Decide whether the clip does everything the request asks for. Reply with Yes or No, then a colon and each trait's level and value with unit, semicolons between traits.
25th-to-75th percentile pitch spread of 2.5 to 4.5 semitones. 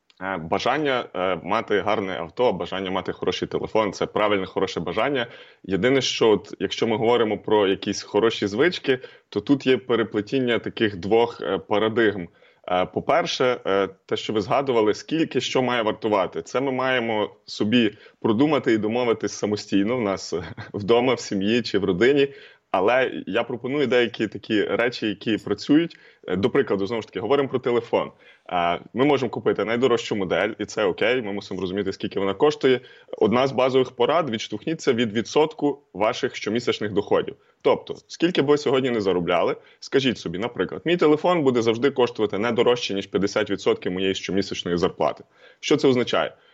No: average, 4.9 semitones